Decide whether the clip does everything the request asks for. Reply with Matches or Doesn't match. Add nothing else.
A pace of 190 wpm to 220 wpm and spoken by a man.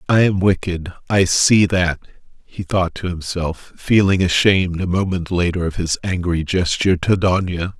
Doesn't match